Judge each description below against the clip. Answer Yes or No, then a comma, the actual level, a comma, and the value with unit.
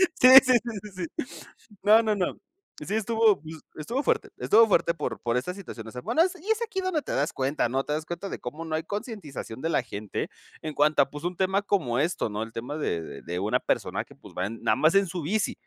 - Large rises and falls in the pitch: Yes, wide, 7.9 semitones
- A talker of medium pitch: Yes, medium, 165 Hz